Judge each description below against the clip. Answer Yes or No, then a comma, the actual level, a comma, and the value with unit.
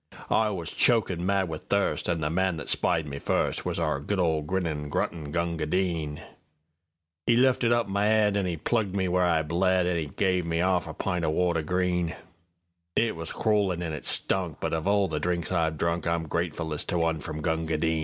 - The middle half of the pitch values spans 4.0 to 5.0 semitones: No, average, 2.7 semitones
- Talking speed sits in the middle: Yes, average, 180 wpm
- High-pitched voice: No, very low, 85 Hz